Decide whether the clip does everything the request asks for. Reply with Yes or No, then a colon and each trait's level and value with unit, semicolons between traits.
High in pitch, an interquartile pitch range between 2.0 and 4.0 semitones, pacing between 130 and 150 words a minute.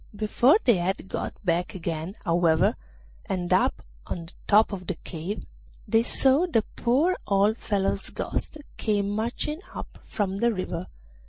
No: high, 200 Hz; average, 4.5 semitones; average, 145 wpm